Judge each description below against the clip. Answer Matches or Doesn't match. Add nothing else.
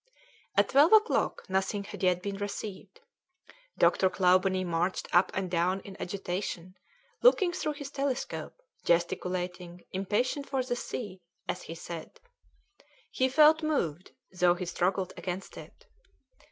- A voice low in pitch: Doesn't match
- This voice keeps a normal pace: Doesn't match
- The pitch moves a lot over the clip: Matches